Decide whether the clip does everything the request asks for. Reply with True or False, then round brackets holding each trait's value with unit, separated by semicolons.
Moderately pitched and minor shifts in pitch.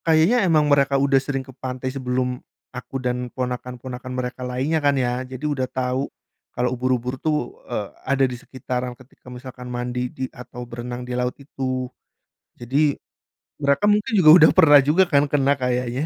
False (130 Hz; 2.1 semitones)